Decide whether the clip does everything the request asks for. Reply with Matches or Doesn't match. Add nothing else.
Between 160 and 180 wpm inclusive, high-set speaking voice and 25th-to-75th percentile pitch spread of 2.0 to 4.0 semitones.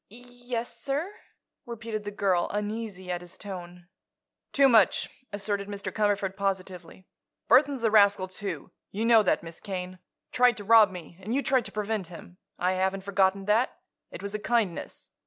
Matches